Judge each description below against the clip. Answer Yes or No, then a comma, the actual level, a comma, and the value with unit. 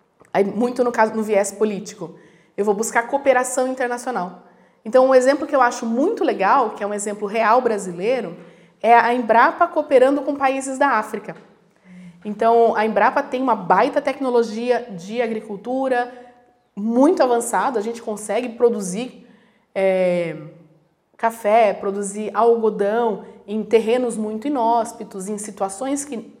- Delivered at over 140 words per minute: No, average, 135 wpm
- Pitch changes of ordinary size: Yes, average, 3.4 semitones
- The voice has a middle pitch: No, high, 225 Hz